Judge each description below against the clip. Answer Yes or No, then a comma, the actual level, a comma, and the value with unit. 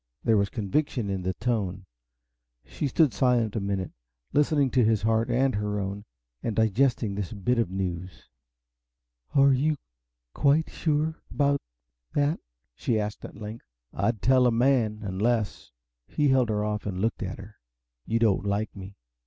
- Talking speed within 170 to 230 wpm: No, average, 160 wpm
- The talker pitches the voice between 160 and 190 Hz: No, low, 110 Hz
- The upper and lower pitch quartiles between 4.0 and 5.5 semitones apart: Yes, average, 4.5 semitones